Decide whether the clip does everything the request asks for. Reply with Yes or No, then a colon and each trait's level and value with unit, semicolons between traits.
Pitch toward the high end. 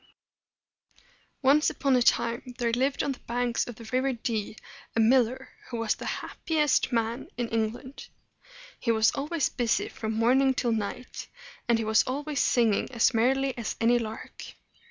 Yes: high, 240 Hz